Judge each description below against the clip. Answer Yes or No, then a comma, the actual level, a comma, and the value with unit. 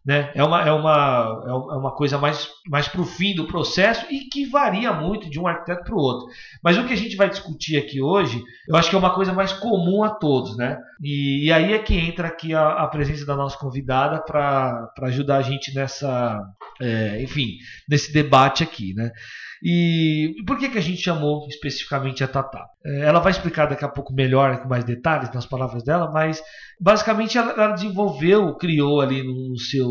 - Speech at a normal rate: No, fast, 205 wpm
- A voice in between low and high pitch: Yes, medium, 150 Hz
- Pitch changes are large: No, average, 4.5 semitones